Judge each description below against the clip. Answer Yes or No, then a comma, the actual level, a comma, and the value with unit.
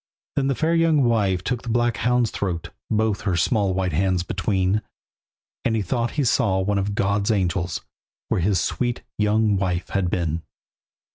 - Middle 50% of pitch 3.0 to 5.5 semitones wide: Yes, average, 4.0 semitones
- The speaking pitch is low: Yes, low, 100 Hz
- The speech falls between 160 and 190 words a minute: Yes, average, 170 wpm